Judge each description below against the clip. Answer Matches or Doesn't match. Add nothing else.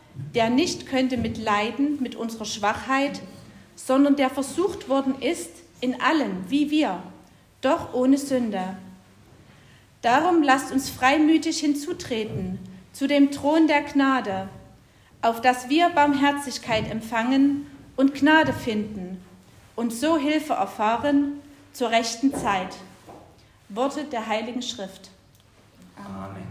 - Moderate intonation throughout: Matches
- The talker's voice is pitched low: Doesn't match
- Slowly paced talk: Matches